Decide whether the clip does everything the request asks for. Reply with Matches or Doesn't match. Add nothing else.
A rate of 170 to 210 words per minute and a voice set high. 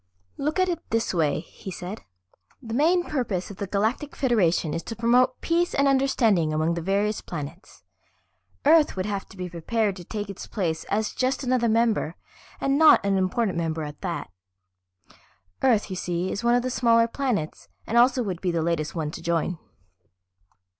Matches